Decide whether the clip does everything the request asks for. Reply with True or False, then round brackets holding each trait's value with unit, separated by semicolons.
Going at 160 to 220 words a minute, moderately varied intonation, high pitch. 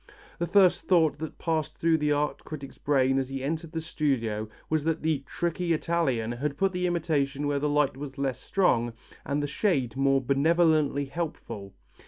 False (180 wpm; 3.3 semitones; 150 Hz)